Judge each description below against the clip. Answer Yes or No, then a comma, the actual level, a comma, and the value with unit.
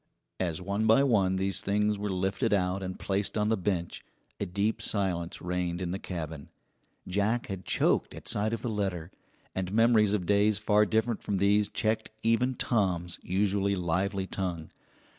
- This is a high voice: No, low, 100 Hz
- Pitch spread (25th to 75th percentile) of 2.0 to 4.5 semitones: Yes, narrow, 2.6 semitones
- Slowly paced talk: No, average, 170 wpm